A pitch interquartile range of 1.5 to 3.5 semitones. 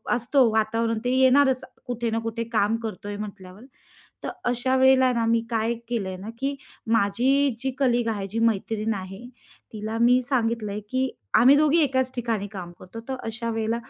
Yes: average, 2.9 semitones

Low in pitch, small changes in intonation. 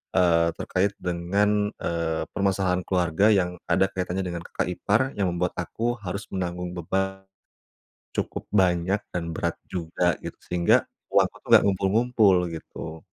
Yes: very low, 90 Hz; narrow, 2.1 semitones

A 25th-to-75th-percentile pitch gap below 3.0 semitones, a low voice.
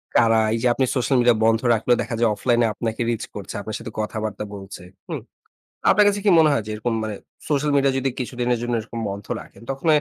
No: average, 3.3 semitones; low, 120 Hz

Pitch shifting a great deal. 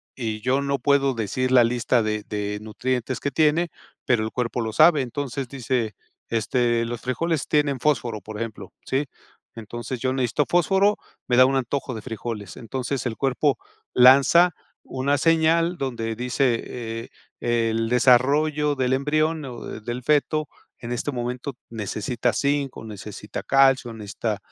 No: average, 3.5 semitones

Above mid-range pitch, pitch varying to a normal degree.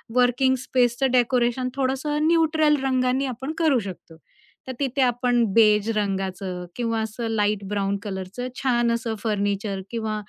Yes: high, 240 Hz; average, 3.9 semitones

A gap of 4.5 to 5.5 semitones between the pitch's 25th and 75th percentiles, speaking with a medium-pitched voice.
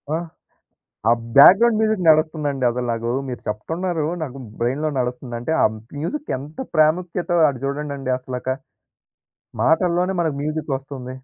Yes: average, 4.9 semitones; medium, 150 Hz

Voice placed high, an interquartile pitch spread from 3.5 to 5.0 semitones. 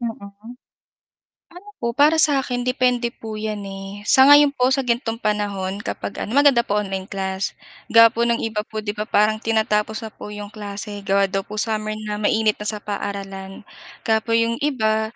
No: high, 215 Hz; narrow, 2.5 semitones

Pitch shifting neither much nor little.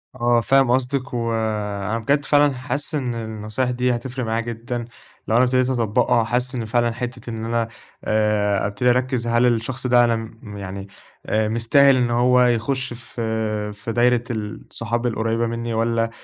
No: narrow, 2.0 semitones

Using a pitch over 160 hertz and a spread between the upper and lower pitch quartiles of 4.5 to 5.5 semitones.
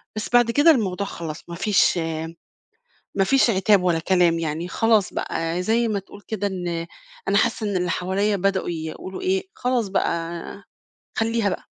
No: high, 190 Hz; average, 3.8 semitones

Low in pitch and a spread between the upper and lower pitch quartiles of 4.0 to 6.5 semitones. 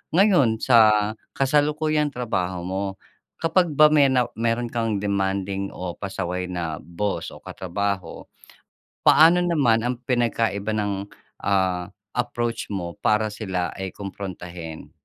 Yes: low, 105 Hz; average, 4.6 semitones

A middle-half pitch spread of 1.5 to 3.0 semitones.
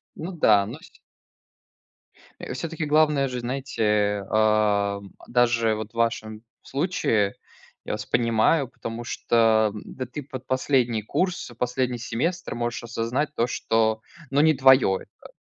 No: average, 3.7 semitones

